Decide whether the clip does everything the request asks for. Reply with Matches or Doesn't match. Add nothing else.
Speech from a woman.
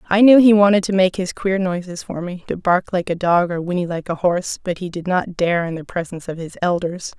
Matches